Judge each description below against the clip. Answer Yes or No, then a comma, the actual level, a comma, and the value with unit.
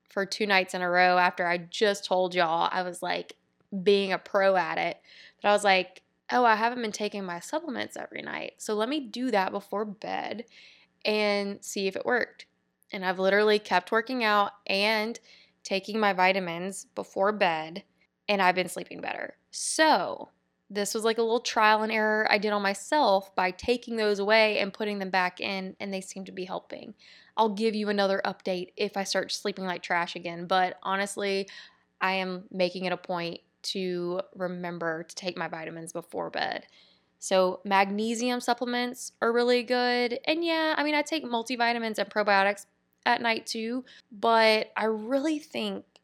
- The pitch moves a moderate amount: Yes, average, 3.3 semitones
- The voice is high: Yes, high, 200 Hz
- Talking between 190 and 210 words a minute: No, average, 180 wpm